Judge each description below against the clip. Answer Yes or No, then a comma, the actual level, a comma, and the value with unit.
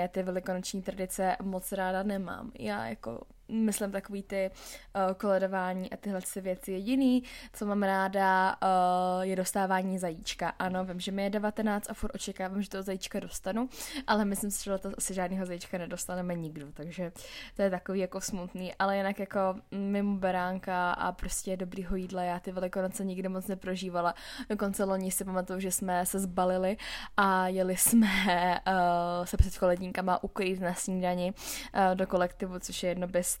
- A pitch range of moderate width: No, narrow, 1.4 semitones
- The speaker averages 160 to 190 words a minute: Yes, fast, 170 wpm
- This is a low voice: No, high, 190 Hz